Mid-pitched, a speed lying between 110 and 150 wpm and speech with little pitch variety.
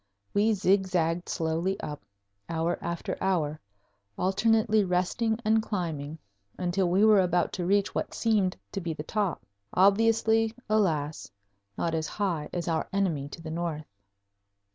No: medium, 180 Hz; average, 140 wpm; average, 3.8 semitones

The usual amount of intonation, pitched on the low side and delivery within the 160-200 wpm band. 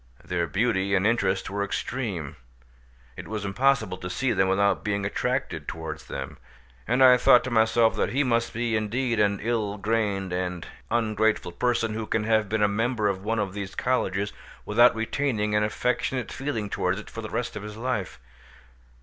Yes: average, 3.0 semitones; low, 110 Hz; average, 180 wpm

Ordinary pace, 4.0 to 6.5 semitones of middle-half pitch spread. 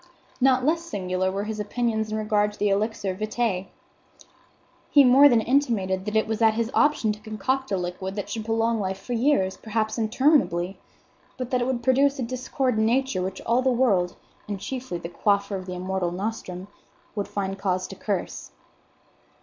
Yes: average, 185 wpm; average, 4.4 semitones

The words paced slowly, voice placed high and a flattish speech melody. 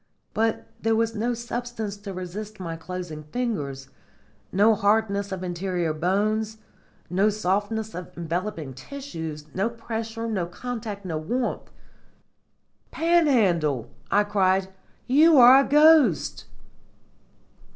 No: slow, 110 wpm; high, 205 Hz; average, 4.3 semitones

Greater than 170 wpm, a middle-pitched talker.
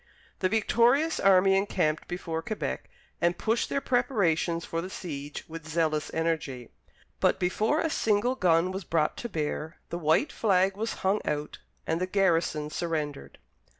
No: average, 150 wpm; medium, 175 Hz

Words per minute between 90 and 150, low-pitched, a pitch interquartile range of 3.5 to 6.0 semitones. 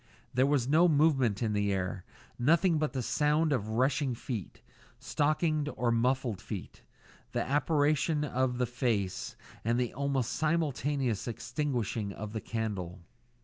Yes: average, 140 wpm; low, 130 Hz; average, 4.7 semitones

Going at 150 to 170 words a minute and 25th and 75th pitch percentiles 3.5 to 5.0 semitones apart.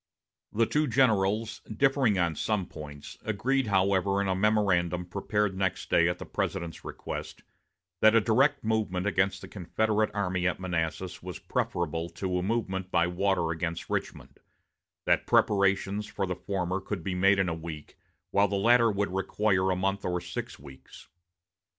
No: average, 165 wpm; average, 2.8 semitones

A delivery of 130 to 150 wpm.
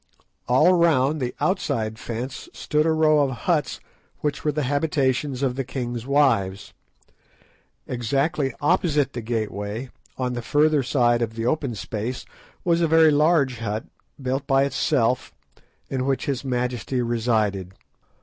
Yes: average, 140 wpm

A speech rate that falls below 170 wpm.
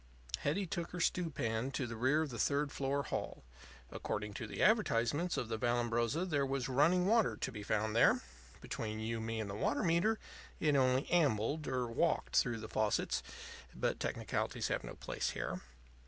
No: average, 185 wpm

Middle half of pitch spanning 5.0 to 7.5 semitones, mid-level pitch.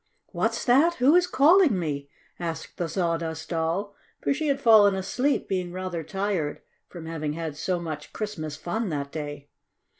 Yes: wide, 5.5 semitones; medium, 175 Hz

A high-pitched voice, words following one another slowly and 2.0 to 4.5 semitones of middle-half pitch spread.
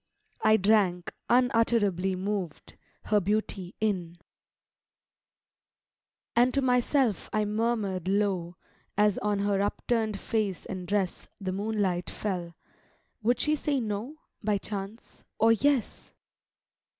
Yes: high, 210 Hz; slow, 115 wpm; average, 3.0 semitones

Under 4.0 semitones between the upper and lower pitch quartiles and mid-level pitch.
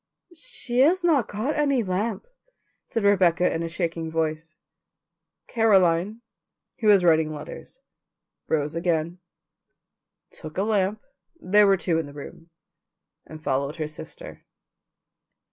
No: average, 4.9 semitones; medium, 180 Hz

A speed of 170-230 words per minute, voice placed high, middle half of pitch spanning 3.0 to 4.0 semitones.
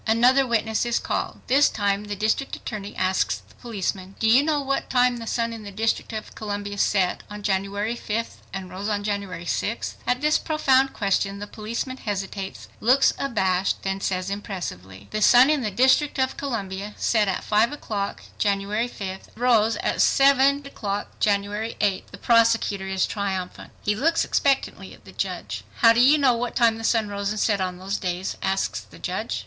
Yes: average, 185 wpm; high, 210 Hz; average, 3.5 semitones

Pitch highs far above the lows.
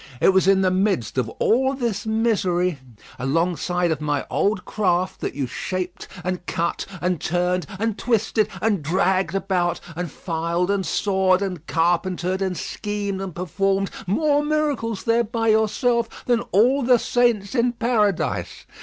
No: average, 4.0 semitones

